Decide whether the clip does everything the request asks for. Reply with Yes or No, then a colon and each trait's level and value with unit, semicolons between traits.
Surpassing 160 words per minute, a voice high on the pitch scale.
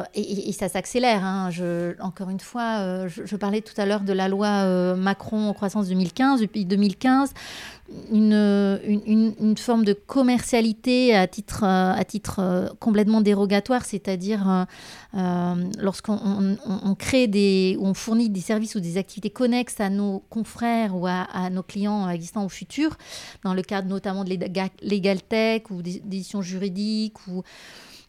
Yes: average, 170 wpm; high, 200 Hz